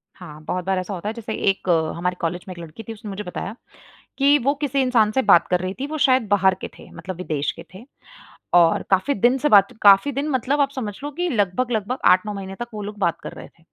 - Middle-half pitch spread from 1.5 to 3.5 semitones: No, wide, 5.5 semitones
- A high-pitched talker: Yes, high, 205 Hz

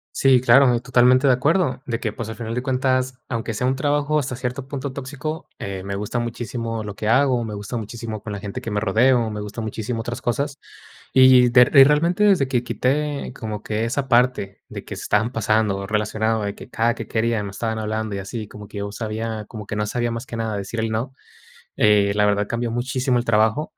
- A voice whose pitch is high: No, low, 115 Hz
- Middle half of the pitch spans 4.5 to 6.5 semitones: No, average, 3.3 semitones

